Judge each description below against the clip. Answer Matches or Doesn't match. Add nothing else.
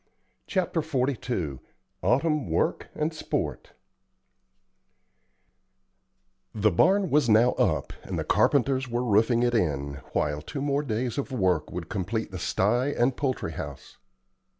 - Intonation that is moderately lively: Doesn't match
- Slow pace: Matches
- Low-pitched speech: Matches